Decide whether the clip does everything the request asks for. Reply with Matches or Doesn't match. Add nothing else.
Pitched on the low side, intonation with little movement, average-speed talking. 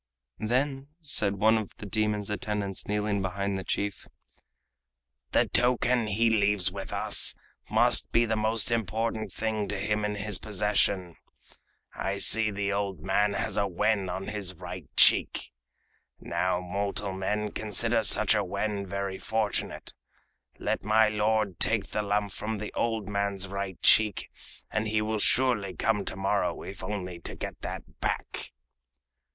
Matches